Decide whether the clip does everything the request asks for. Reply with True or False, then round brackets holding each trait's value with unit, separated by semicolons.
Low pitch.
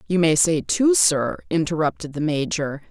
False (160 Hz)